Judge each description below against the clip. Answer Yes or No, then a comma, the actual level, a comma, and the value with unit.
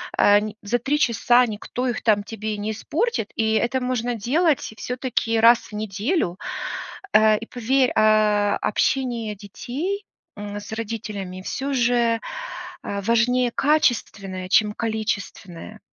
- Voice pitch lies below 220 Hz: No, high, 225 Hz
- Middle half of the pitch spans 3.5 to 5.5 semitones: No, average, 3.1 semitones